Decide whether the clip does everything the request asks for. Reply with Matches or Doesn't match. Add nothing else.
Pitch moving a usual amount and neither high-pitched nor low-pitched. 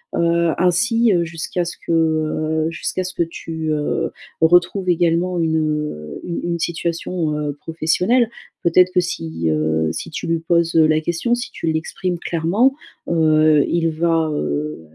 Doesn't match